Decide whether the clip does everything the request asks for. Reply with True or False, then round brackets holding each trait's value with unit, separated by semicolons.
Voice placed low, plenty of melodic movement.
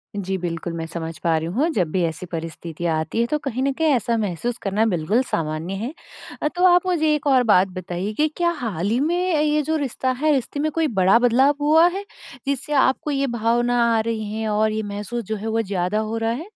False (225 Hz; 7.3 semitones)